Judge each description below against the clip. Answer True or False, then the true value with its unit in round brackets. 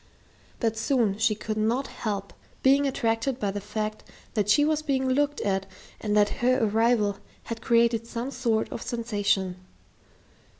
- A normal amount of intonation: True (3.4 semitones)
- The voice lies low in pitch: False (225 Hz)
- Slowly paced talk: False (155 wpm)